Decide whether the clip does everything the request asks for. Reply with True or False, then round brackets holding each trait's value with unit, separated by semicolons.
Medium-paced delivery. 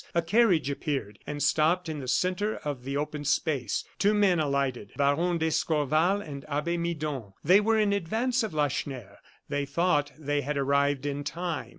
True (170 wpm)